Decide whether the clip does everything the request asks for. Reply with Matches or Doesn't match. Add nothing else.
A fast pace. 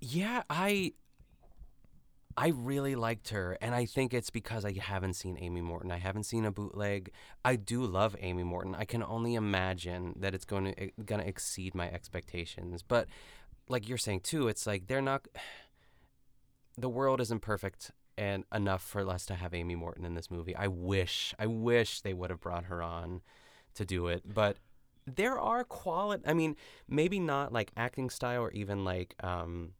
Doesn't match